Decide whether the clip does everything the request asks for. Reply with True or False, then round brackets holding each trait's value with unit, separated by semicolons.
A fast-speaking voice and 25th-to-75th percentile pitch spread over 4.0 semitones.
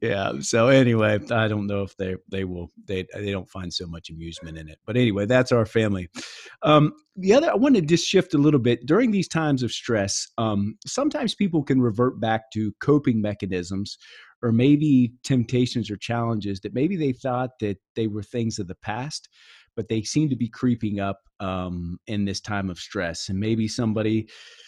False (195 wpm; 4.6 semitones)